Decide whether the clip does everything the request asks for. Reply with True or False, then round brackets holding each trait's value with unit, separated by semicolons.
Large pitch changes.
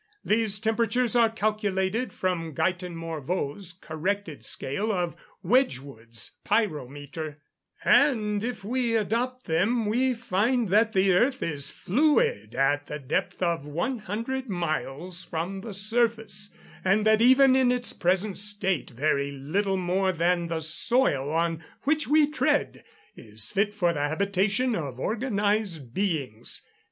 True (5.8 semitones)